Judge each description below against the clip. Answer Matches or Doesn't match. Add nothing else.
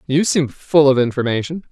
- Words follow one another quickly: Doesn't match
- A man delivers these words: Matches